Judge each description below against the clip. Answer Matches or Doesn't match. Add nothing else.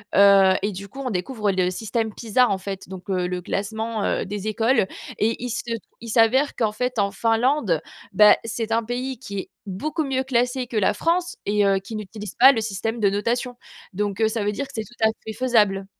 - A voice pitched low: Doesn't match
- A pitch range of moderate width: Matches